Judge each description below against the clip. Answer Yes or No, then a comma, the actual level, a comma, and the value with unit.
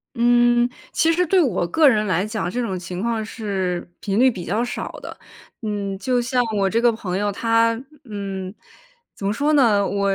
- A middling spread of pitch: Yes, average, 3.5 semitones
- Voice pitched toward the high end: Yes, high, 215 Hz